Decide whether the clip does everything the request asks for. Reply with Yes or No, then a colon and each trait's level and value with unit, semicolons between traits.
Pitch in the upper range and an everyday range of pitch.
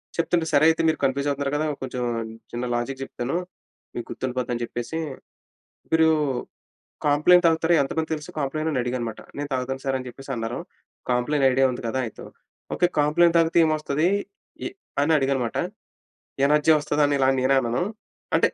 No: medium, 140 Hz; average, 3.5 semitones